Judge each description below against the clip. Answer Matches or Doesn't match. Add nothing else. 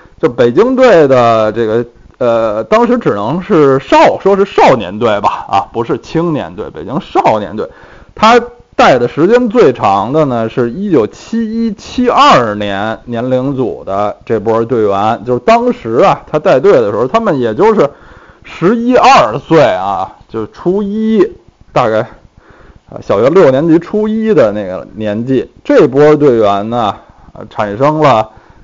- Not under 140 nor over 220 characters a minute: Matches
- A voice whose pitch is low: Doesn't match